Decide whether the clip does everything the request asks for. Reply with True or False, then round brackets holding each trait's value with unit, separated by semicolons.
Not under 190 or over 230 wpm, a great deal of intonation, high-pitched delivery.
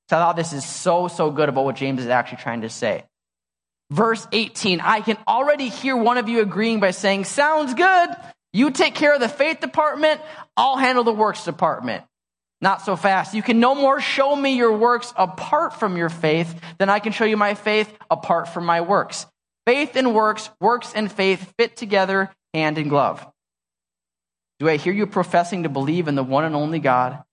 True (200 wpm; 7.5 semitones; 195 Hz)